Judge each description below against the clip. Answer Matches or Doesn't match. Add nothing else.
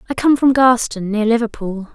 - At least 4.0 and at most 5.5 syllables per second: Matches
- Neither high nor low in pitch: Doesn't match